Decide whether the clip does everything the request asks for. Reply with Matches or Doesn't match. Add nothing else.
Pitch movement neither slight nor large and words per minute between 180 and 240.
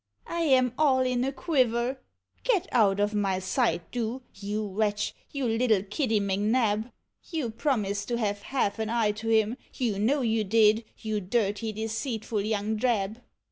Doesn't match